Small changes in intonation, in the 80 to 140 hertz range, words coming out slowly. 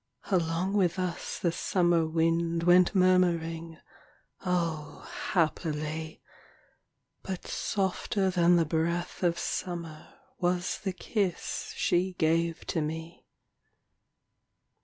No: narrow, 1.9 semitones; medium, 170 Hz; slow, 105 wpm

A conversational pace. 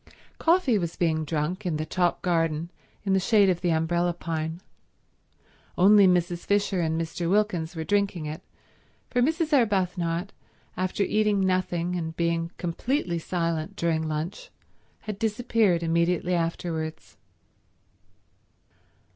No: slow, 125 wpm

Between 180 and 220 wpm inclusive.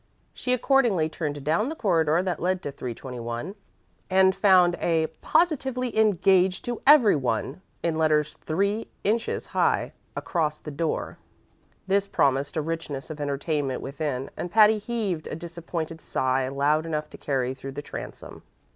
No: average, 145 wpm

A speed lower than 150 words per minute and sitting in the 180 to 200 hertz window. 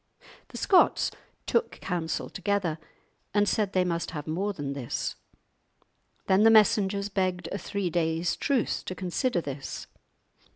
Yes: slow, 135 wpm; medium, 185 Hz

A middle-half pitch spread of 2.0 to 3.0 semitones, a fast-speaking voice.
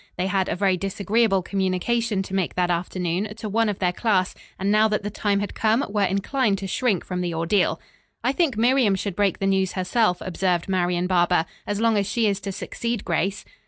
Yes: average, 2.7 semitones; fast, 210 wpm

